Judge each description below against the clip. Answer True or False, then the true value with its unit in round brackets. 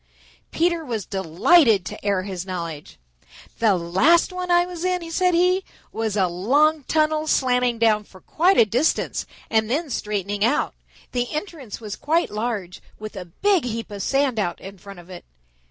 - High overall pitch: True (230 Hz)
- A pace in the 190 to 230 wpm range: False (170 wpm)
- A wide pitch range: True (8.1 semitones)